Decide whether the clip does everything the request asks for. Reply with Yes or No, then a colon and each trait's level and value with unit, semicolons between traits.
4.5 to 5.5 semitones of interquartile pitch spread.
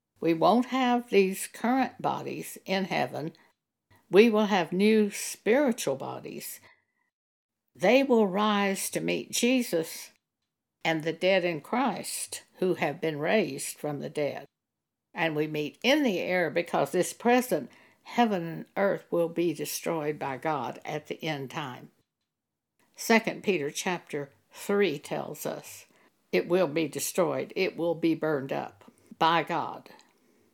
Yes: average, 5.1 semitones